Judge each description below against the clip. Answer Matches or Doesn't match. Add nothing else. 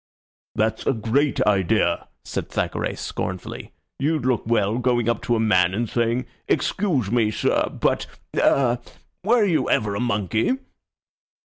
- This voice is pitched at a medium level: Doesn't match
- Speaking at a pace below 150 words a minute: Matches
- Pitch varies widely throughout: Doesn't match